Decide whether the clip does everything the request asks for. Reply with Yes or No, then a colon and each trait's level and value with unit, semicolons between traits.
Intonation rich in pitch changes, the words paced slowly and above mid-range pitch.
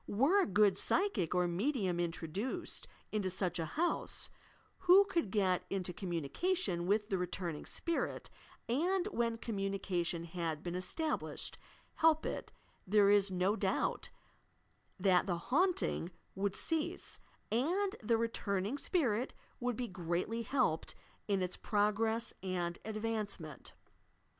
Yes: wide, 5.8 semitones; slow, 130 wpm; high, 205 Hz